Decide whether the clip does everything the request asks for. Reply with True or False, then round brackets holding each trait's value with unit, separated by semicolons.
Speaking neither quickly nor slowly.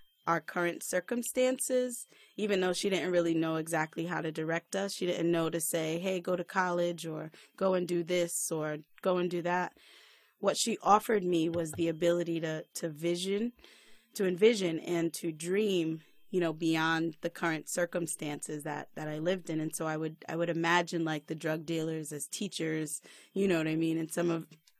True (195 wpm)